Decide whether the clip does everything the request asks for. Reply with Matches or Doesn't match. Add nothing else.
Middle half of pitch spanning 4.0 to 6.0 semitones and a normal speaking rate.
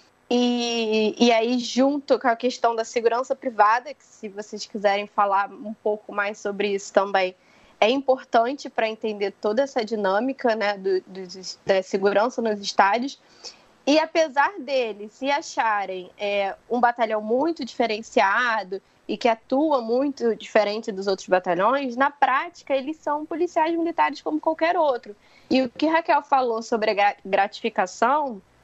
Matches